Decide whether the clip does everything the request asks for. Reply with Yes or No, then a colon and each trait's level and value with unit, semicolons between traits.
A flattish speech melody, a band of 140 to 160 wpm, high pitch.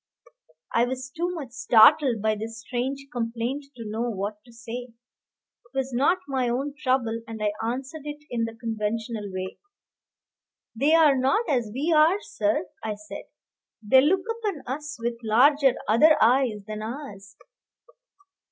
No: average, 3.8 semitones; average, 150 wpm; high, 245 Hz